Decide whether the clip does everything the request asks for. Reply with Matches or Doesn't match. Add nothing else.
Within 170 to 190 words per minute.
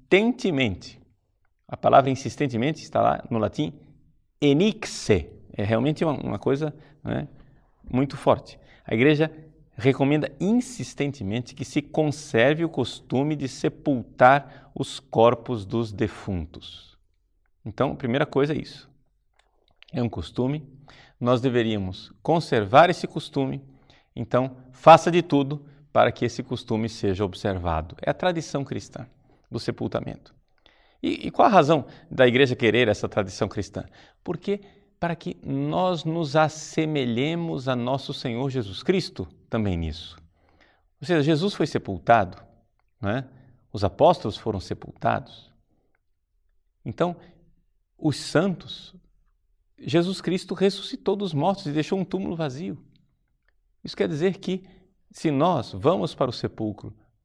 Doesn't match